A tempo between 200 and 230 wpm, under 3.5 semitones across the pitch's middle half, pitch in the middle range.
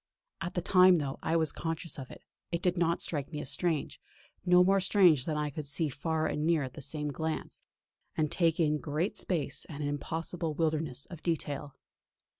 Yes: fast, 205 wpm; narrow, 2.6 semitones; medium, 160 Hz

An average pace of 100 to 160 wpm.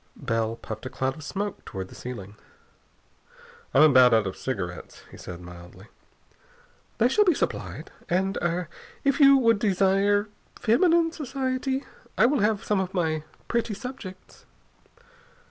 Yes: average, 145 wpm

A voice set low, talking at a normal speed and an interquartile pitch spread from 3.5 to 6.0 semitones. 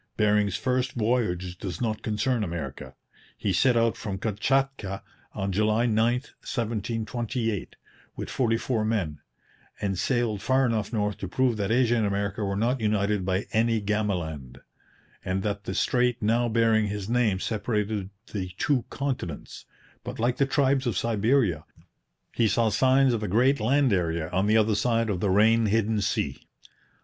No: low, 110 Hz; average, 160 wpm; average, 3.1 semitones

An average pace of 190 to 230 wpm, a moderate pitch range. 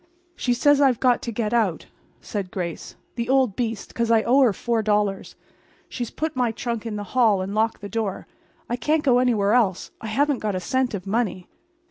Yes: average, 200 wpm; average, 3.3 semitones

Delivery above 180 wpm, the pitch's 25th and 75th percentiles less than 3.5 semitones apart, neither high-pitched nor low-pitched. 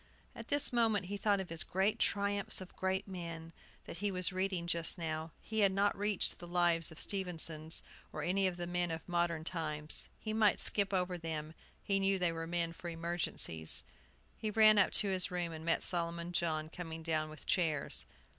Yes: average, 200 wpm; average, 2.9 semitones; medium, 175 Hz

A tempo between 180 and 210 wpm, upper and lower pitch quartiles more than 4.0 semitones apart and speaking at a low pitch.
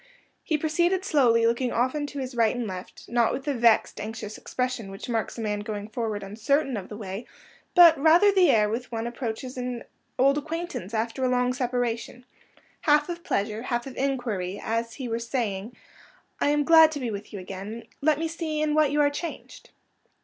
No: average, 200 wpm; average, 4.8 semitones; high, 245 Hz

